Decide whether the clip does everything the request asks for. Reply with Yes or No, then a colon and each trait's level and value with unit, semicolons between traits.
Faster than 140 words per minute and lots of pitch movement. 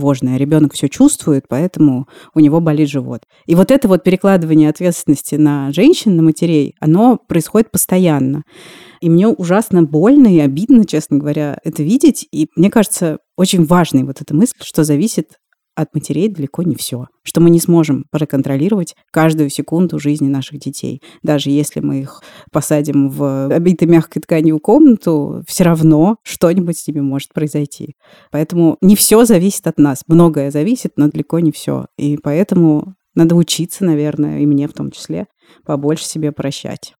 No: fast, 160 wpm; average, 3.4 semitones